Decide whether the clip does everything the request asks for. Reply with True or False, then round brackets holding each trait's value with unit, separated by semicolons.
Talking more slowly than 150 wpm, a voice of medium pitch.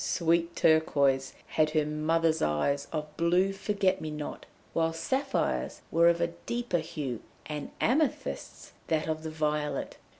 True (135 wpm; 160 Hz)